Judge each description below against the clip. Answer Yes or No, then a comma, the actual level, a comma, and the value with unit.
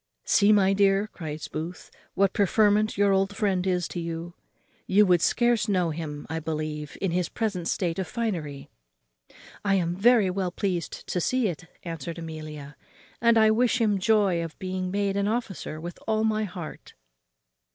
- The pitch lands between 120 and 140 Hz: No, medium, 185 Hz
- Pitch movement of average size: Yes, average, 3.8 semitones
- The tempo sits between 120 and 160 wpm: No, average, 170 wpm